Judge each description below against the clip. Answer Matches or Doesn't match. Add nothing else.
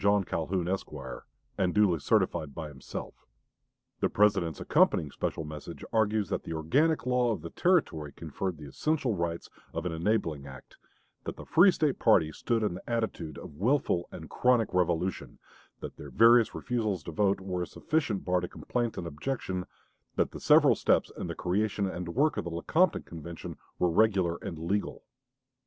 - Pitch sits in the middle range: Doesn't match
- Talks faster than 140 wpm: Matches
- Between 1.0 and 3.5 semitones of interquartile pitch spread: Doesn't match